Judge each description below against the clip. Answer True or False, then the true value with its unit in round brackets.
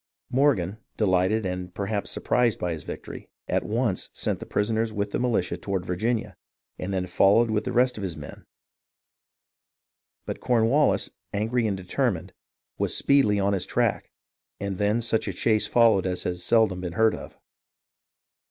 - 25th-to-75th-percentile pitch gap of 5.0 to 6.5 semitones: False (3.7 semitones)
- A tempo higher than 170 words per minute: False (160 wpm)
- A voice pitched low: True (105 Hz)